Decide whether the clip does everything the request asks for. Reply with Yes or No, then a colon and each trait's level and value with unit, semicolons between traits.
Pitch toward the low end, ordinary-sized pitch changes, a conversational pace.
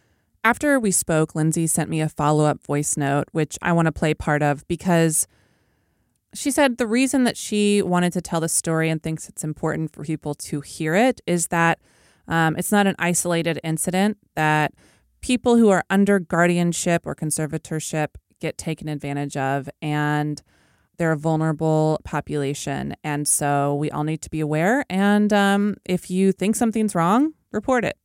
No: medium, 165 Hz; average, 4.3 semitones; average, 175 wpm